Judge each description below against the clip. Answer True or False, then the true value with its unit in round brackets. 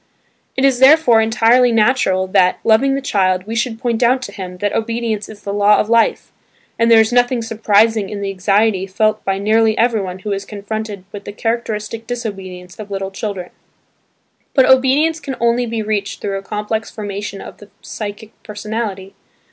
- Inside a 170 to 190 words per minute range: True (180 wpm)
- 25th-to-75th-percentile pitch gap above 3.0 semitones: False (2.6 semitones)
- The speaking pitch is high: True (215 Hz)